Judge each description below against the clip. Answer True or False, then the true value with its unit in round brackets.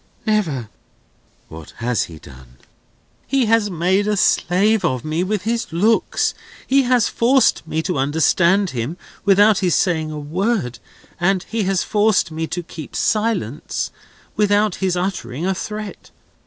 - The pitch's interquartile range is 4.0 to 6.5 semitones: True (5.2 semitones)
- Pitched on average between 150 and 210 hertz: True (185 Hz)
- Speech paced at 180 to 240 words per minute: False (145 wpm)